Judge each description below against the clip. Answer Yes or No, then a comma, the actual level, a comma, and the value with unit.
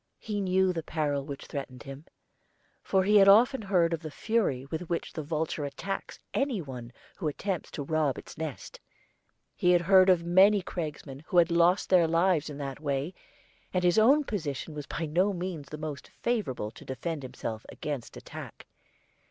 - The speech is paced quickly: No, average, 180 wpm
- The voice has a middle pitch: Yes, medium, 165 Hz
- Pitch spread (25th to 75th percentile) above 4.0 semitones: Yes, average, 4.7 semitones